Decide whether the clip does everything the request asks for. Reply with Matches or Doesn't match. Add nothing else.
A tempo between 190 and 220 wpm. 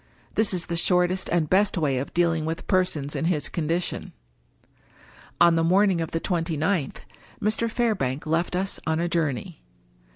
Doesn't match